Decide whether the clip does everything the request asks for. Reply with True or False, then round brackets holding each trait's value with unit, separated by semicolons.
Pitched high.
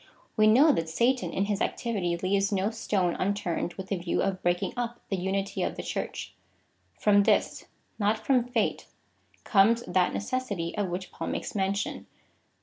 True (200 Hz)